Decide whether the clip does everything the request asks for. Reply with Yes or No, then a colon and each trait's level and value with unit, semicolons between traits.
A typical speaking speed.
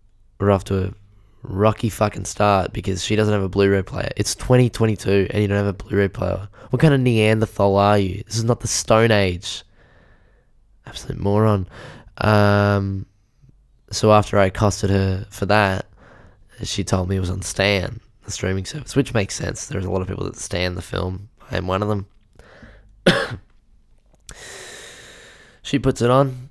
Yes: average, 175 wpm